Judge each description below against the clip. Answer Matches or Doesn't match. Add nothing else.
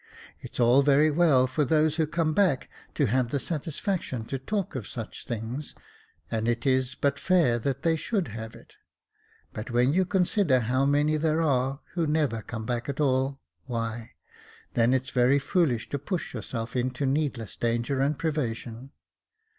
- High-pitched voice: Doesn't match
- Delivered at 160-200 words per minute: Matches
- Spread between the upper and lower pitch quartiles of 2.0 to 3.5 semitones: Doesn't match